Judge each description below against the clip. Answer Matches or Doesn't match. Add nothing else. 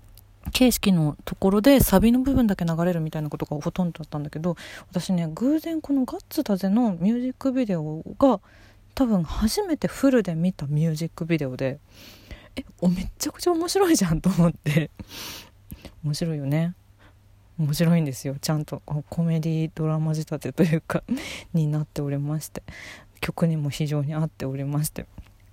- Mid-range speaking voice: Matches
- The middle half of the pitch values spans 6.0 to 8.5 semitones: Doesn't match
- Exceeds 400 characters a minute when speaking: Doesn't match